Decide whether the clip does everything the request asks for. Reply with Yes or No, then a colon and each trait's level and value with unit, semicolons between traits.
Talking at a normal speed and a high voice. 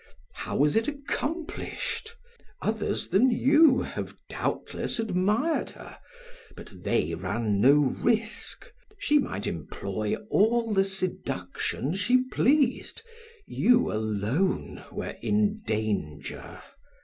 No: slow, 100 wpm; high, 205 Hz